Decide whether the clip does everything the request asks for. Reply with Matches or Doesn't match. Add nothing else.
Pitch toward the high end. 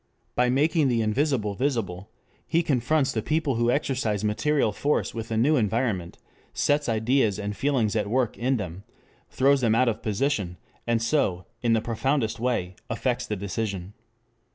Doesn't match